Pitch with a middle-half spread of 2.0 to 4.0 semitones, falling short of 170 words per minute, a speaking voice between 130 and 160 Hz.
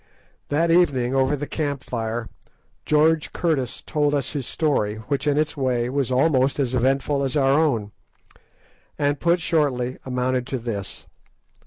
Yes: average, 2.9 semitones; average, 150 wpm; low, 135 Hz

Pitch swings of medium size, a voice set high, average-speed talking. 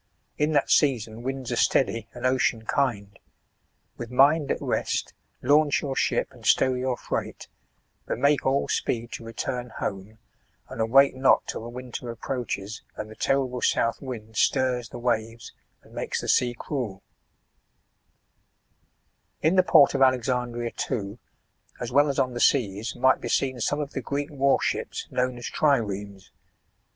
No: average, 3.0 semitones; low, 125 Hz; average, 160 wpm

